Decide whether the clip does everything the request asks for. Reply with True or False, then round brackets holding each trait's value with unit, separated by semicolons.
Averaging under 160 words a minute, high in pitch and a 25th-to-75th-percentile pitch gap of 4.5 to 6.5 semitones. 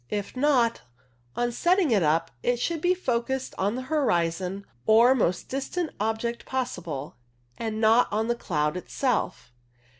True (145 wpm; 230 Hz; 5.6 semitones)